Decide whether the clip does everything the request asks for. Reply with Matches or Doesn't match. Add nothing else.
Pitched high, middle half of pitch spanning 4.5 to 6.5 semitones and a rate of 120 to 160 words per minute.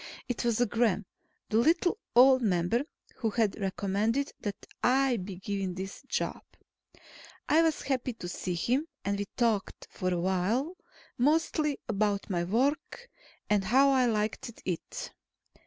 Matches